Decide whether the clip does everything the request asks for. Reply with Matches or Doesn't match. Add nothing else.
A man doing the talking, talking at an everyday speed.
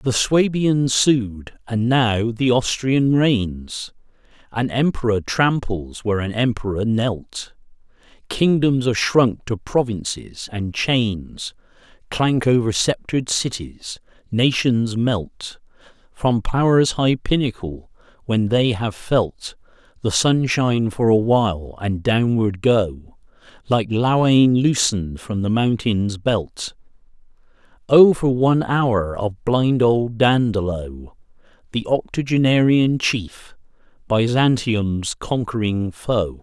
Doesn't match